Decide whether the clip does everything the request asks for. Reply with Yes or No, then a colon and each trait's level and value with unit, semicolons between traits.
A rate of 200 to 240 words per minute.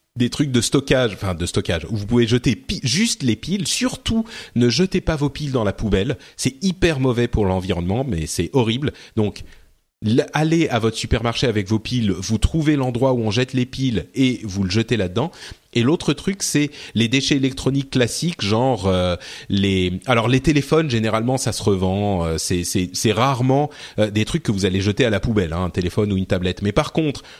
Yes: average, 210 wpm